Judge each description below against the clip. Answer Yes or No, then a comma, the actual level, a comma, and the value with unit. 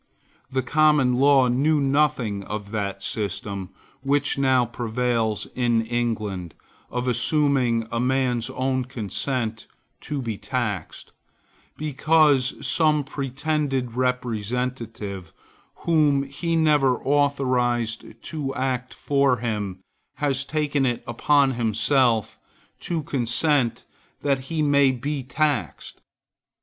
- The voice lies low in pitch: Yes, low, 130 Hz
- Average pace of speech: No, slow, 105 wpm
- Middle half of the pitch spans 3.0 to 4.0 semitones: Yes, average, 3.5 semitones